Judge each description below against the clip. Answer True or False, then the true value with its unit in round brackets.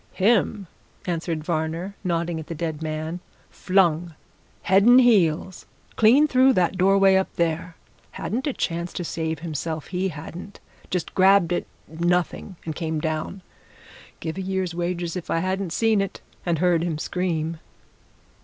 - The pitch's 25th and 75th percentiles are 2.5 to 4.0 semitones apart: True (2.9 semitones)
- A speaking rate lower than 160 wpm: True (150 wpm)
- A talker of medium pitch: True (175 Hz)